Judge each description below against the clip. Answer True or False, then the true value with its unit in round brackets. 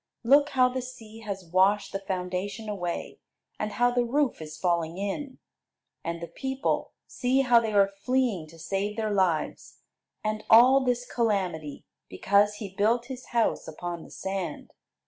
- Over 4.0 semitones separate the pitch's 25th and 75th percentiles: True (4.9 semitones)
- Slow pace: False (160 wpm)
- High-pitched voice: True (210 Hz)